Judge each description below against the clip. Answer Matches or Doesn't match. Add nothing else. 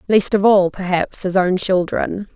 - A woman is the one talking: Matches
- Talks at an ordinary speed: Matches